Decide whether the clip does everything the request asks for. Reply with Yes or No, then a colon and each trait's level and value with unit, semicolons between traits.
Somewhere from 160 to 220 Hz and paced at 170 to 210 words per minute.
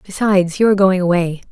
Yes: medium, 185 Hz; average, 200 wpm